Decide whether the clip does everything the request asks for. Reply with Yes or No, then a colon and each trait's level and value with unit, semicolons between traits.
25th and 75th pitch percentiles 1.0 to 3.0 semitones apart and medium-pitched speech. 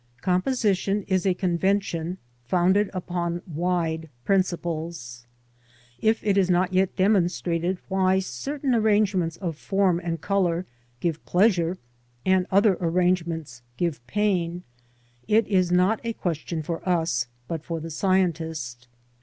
Yes: narrow, 2.6 semitones; medium, 180 Hz